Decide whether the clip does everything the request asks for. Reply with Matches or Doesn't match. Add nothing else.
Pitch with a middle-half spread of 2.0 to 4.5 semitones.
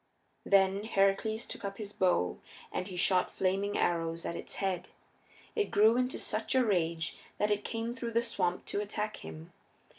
Matches